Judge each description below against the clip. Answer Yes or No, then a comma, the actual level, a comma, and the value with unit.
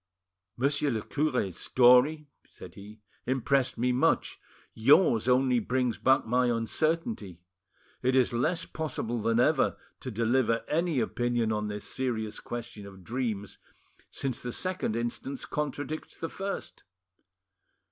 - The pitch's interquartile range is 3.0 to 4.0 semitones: Yes, average, 3.5 semitones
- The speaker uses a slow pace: Yes, slow, 125 wpm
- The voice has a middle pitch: No, low, 125 Hz